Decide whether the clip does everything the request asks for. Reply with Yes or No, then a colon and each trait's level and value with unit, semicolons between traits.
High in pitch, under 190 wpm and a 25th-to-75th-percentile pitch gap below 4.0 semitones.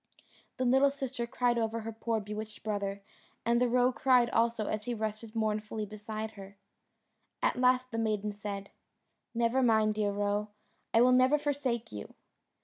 Yes: high, 225 Hz; average, 160 wpm; narrow, 2.6 semitones